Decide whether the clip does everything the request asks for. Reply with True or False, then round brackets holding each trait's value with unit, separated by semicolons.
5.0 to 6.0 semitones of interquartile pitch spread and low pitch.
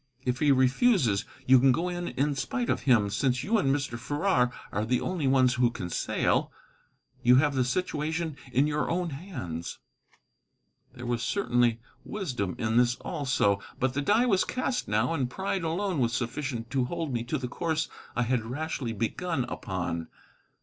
True (5.3 semitones; 130 Hz)